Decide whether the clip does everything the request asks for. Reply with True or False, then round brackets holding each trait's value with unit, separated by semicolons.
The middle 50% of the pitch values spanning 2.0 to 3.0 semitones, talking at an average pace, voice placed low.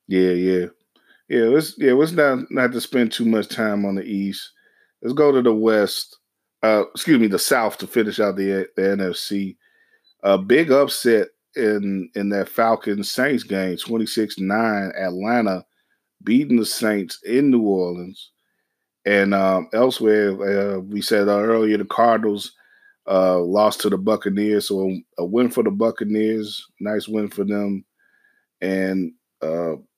True (2.7 semitones; 150 wpm; 105 Hz)